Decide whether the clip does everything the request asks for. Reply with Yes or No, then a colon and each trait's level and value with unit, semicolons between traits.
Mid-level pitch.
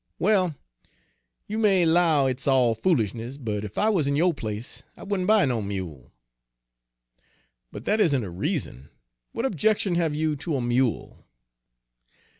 Yes: medium, 145 Hz